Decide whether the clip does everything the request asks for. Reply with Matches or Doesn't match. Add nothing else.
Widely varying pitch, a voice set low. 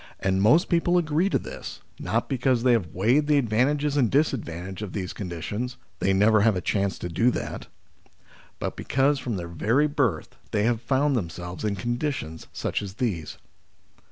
Matches